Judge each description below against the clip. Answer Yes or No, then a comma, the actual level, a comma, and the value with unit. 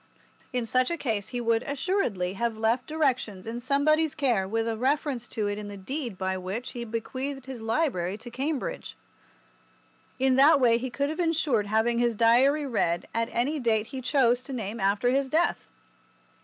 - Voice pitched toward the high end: Yes, high, 240 Hz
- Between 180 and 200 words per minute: Yes, average, 185 wpm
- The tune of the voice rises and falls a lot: No, average, 3.8 semitones